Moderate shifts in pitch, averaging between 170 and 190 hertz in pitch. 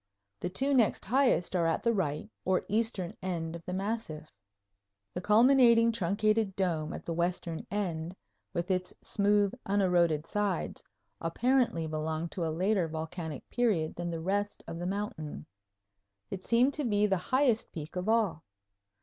Yes: average, 4.6 semitones; medium, 185 Hz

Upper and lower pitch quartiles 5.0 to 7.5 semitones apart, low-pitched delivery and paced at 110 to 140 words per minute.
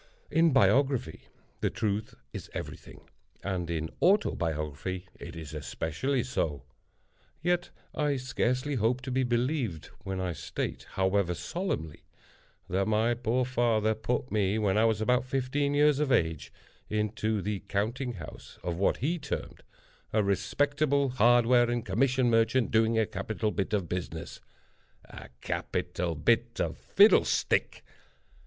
Yes: wide, 5.4 semitones; low, 115 Hz; slow, 135 wpm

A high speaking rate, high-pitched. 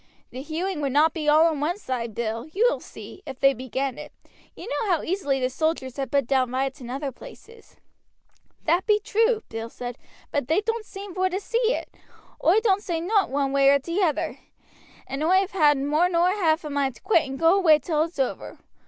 Yes: fast, 220 wpm; very high, 315 Hz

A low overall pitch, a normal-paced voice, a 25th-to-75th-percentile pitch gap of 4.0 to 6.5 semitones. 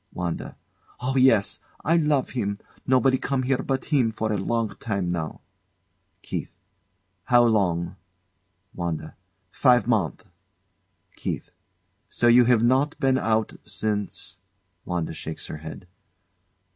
No: low, 115 Hz; slow, 120 wpm; average, 4.8 semitones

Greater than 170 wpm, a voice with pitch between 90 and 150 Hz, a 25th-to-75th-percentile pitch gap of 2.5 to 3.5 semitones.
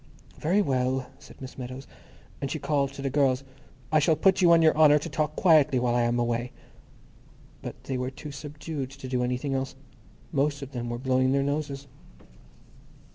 Yes: average, 185 wpm; low, 135 Hz; average, 2.8 semitones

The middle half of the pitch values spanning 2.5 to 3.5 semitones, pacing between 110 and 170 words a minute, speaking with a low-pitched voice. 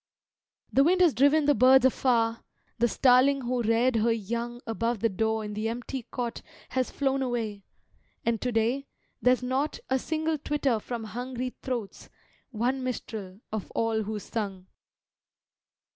No: average, 2.8 semitones; average, 150 wpm; high, 240 Hz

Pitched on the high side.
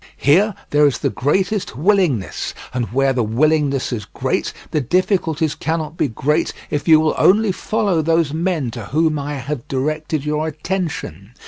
No: medium, 155 Hz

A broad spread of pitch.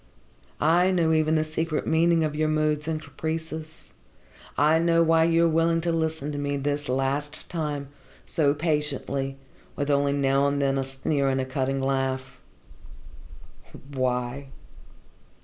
No: average, 2.7 semitones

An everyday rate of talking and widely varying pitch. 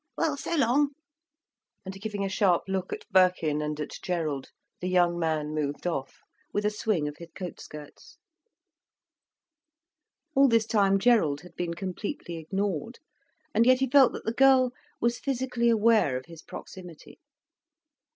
Yes: average, 150 wpm; wide, 6.2 semitones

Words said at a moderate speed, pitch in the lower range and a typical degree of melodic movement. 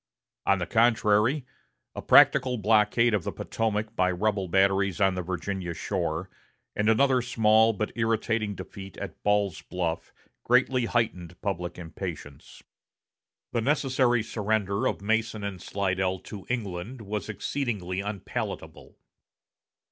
No: slow, 125 wpm; low, 105 Hz; average, 3.3 semitones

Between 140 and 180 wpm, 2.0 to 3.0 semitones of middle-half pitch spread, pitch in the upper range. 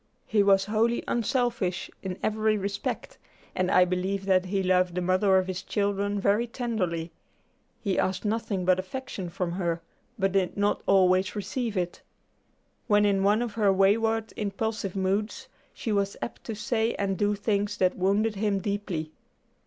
Yes: average, 160 wpm; narrow, 2.5 semitones; high, 200 Hz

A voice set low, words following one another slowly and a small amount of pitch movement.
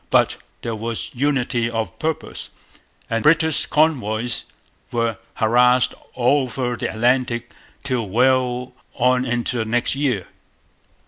Yes: low, 125 Hz; slow, 120 wpm; narrow, 2.1 semitones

